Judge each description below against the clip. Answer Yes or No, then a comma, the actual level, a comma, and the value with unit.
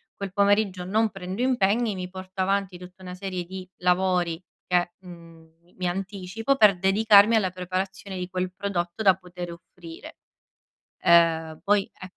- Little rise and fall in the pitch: Yes, narrow, 1.9 semitones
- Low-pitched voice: No, medium, 185 Hz